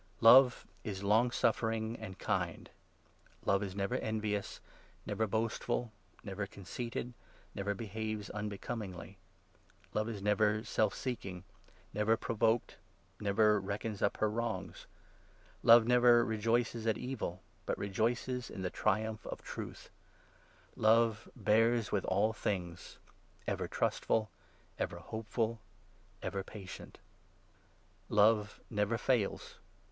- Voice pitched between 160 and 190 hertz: No, low, 110 Hz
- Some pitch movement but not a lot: No, narrow, 2.1 semitones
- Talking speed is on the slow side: Yes, slow, 120 wpm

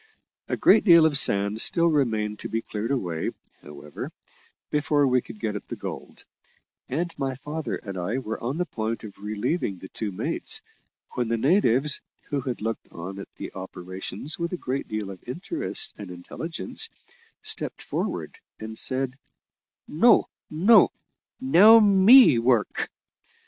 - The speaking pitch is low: Yes, low, 125 Hz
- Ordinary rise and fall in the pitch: No, wide, 7.3 semitones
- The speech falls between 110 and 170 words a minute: Yes, average, 155 wpm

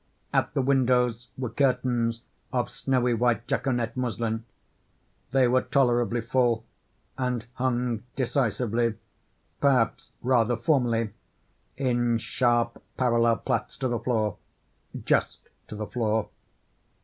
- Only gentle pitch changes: Yes, narrow, 1.7 semitones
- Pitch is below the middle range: Yes, low, 120 Hz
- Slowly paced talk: Yes, slow, 105 wpm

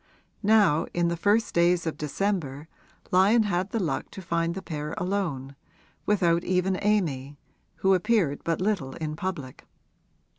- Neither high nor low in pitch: Yes, medium, 175 Hz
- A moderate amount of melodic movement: Yes, average, 4.4 semitones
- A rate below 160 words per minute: Yes, average, 145 wpm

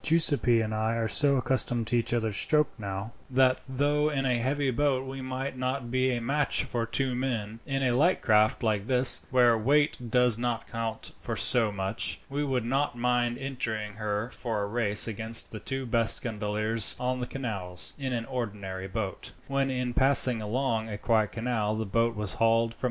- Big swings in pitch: No, average, 3.1 semitones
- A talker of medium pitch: No, low, 120 Hz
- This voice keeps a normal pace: Yes, average, 160 wpm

